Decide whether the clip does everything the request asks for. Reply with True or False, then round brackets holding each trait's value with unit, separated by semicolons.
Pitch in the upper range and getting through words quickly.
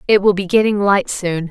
True (195 Hz; 240 wpm)